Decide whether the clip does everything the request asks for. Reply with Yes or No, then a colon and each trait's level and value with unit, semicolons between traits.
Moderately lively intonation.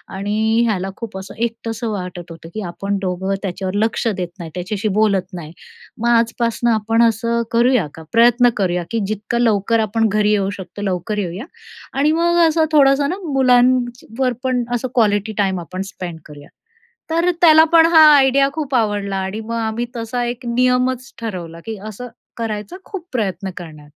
Yes: average, 4.1 semitones